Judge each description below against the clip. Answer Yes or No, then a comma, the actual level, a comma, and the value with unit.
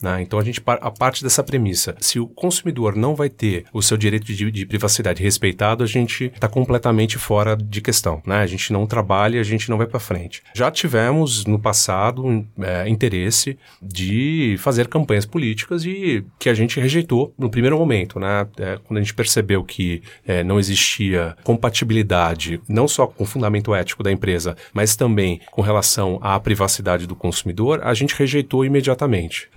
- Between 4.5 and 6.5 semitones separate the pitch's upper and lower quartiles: No, average, 4.1 semitones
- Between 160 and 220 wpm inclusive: Yes, average, 180 wpm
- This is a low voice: Yes, low, 110 Hz